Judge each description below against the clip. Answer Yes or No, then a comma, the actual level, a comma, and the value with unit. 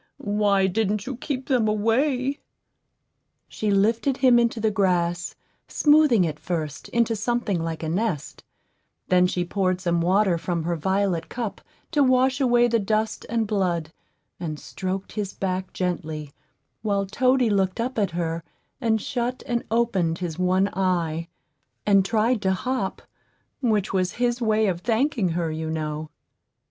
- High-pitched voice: Yes, high, 200 Hz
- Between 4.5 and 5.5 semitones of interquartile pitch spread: Yes, average, 4.9 semitones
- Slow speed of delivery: No, average, 150 wpm